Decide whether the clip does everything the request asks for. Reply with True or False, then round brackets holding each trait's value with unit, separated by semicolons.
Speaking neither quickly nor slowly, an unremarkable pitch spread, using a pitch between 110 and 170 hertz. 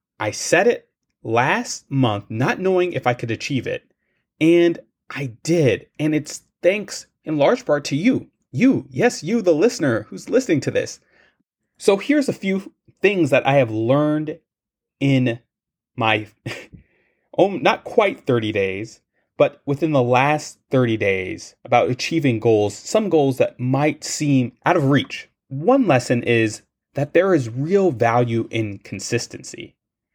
False (150 wpm; 6.4 semitones; 140 Hz)